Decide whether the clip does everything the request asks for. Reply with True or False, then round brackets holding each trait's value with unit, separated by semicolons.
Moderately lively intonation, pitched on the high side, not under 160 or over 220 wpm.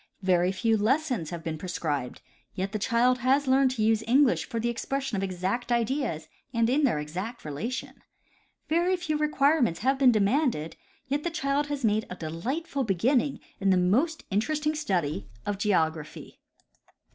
False (6.9 semitones; 230 Hz; 170 wpm)